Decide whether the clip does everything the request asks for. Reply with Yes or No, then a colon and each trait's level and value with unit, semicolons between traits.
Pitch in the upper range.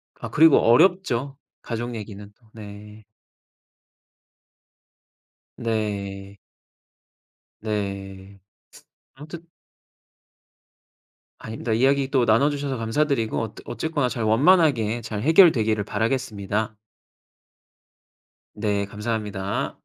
No: low, 110 Hz